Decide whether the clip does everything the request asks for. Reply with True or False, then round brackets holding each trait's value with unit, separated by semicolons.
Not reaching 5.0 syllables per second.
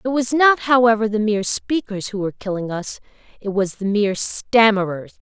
False (5.4 syllables/s)